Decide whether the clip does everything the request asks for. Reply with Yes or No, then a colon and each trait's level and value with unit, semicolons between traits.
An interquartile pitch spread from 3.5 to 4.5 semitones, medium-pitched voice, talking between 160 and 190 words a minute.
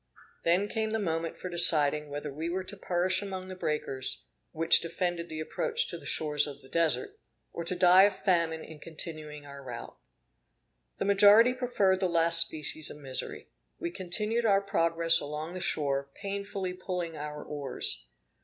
Yes: average, 3.9 semitones; medium, 170 Hz; average, 170 wpm